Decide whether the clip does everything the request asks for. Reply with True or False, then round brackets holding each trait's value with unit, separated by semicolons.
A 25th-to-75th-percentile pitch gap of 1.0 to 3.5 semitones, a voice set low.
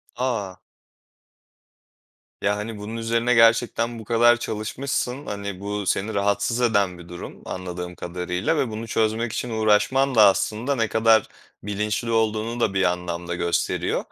True (2.8 semitones; 110 Hz)